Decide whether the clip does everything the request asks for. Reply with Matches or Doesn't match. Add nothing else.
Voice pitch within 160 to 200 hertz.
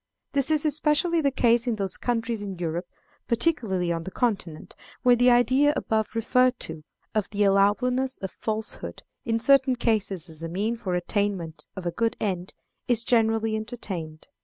Doesn't match